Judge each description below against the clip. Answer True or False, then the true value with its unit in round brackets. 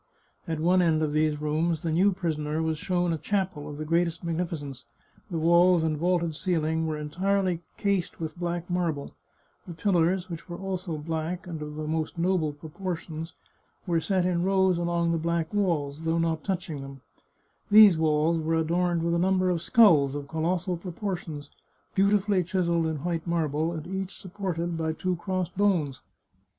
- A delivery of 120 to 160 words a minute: False (175 wpm)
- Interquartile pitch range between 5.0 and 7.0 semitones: False (2.4 semitones)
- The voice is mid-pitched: True (170 Hz)